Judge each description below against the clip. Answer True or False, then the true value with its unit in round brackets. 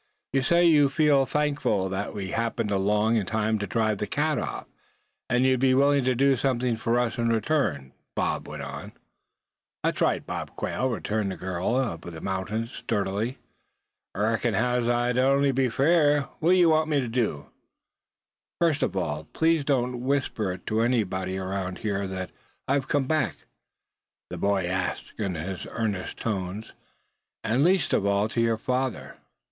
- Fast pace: False (170 wpm)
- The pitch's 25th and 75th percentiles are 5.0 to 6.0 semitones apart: True (5.3 semitones)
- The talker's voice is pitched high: False (115 Hz)